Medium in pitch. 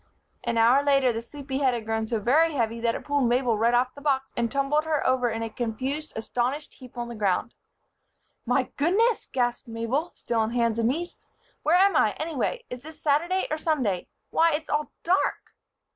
No: very high, 260 Hz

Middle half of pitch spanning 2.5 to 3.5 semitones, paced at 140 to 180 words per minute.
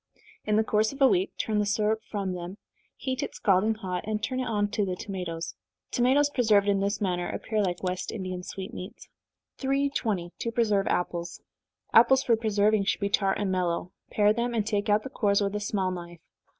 No: average, 3.0 semitones; average, 200 wpm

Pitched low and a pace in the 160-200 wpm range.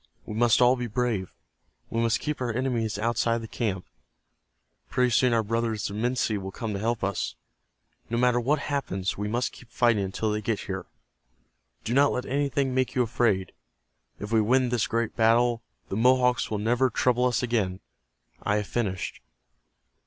Yes: low, 115 Hz; average, 180 wpm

